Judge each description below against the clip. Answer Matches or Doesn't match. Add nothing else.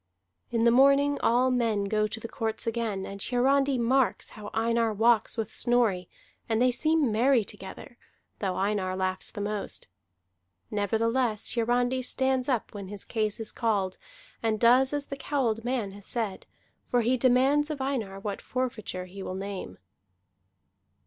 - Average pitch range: Matches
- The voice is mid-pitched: Doesn't match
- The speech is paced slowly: Doesn't match